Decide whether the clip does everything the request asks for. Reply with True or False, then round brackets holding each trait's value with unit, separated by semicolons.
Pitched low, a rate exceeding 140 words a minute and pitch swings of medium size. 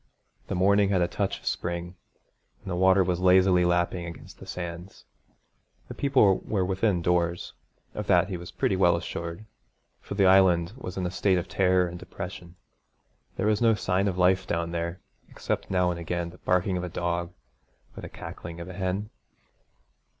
False (90 Hz; 185 wpm; 1.7 semitones)